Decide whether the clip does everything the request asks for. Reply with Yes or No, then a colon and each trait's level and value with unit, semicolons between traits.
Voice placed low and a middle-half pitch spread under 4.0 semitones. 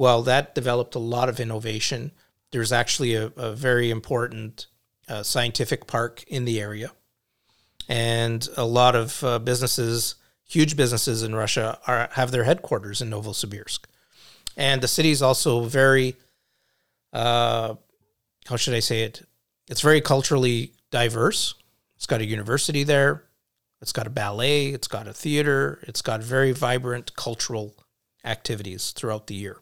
Yes: low, 120 Hz; narrow, 2.5 semitones